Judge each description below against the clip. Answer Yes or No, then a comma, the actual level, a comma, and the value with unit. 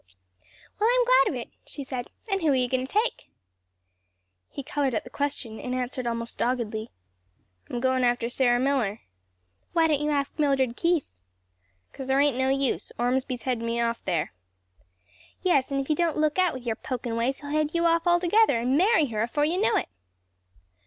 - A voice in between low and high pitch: No, very high, 265 Hz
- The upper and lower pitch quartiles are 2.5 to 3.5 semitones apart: No, average, 4.2 semitones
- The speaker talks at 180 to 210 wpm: Yes, average, 195 wpm